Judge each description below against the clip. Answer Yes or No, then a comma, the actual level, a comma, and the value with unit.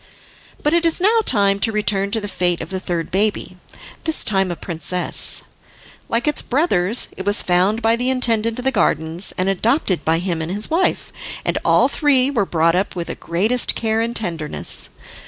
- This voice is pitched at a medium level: No, high, 205 Hz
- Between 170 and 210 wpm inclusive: Yes, average, 190 wpm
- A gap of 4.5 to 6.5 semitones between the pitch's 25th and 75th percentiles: Yes, average, 5.1 semitones